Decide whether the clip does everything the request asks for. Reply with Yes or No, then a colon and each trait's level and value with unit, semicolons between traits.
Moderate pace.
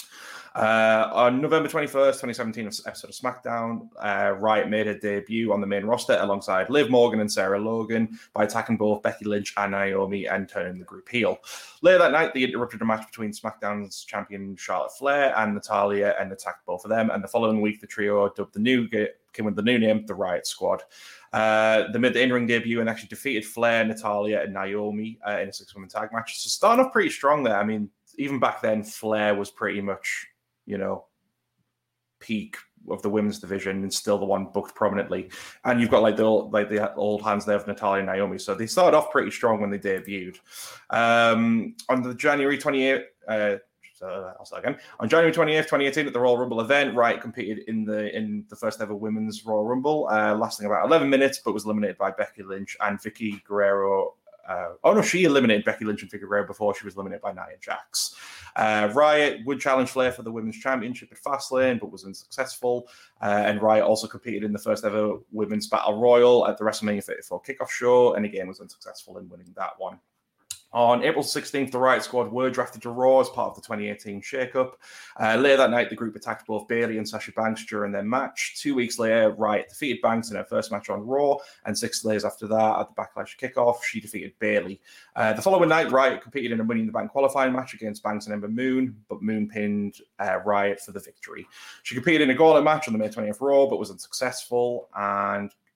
No: fast, 215 wpm